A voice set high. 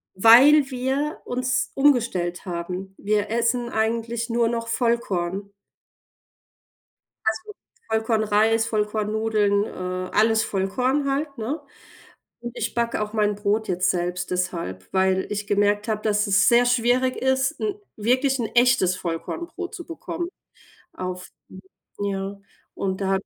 Yes: high, 220 Hz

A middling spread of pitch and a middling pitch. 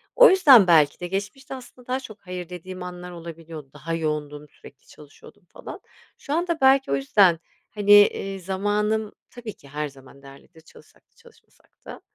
No: wide, 5.9 semitones; medium, 180 Hz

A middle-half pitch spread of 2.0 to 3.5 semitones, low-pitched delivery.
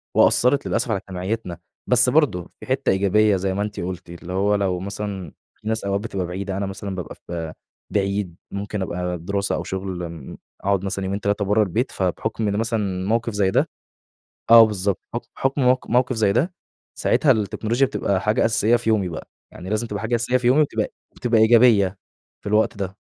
Yes: average, 3.1 semitones; low, 100 Hz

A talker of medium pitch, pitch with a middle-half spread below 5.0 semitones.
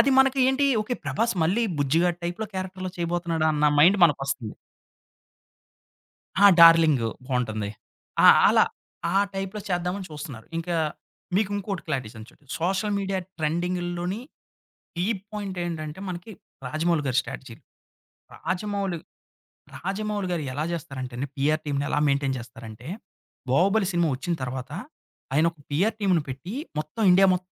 No: medium, 170 Hz; average, 5.3 semitones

